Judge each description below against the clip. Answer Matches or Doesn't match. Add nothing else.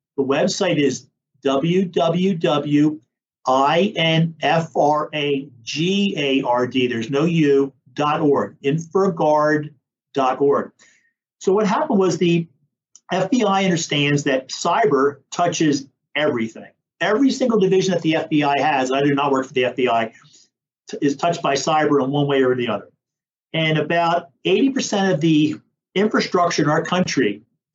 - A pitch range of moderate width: Matches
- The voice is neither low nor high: Matches